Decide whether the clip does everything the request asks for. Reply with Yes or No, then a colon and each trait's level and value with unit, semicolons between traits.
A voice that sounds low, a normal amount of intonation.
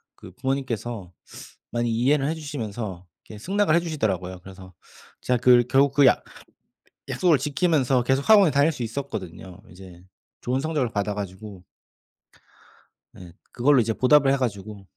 No: low, 120 Hz; wide, 6.0 semitones